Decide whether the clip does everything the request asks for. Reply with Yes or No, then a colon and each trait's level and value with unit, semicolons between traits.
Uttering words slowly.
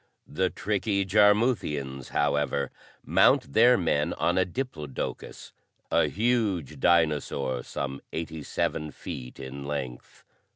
Yes: slow, 110 wpm